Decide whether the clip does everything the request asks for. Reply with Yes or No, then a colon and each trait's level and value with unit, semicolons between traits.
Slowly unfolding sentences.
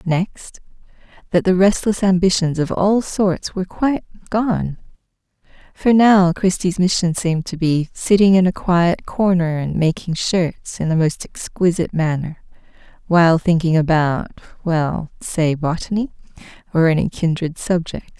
Yes: slow, 130 wpm